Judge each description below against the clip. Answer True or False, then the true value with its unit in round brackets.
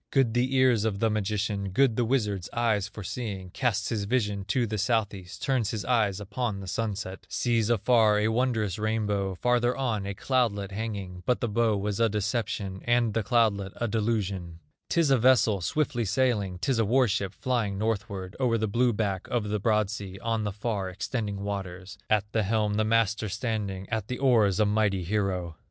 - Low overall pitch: True (105 Hz)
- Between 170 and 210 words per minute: True (190 wpm)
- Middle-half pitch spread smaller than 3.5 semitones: True (2.9 semitones)